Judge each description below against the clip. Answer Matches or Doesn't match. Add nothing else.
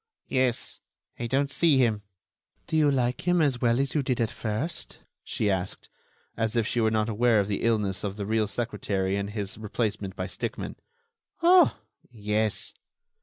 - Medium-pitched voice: Doesn't match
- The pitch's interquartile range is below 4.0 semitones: Matches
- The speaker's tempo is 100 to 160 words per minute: Doesn't match